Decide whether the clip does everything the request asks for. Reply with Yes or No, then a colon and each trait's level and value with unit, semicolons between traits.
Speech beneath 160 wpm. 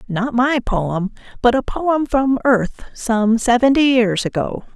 Yes: average, 140 wpm